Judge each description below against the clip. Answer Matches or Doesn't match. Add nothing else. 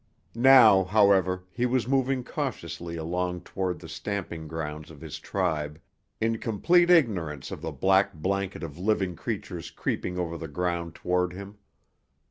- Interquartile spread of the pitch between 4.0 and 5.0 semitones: Matches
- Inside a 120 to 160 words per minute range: Matches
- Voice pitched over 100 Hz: Doesn't match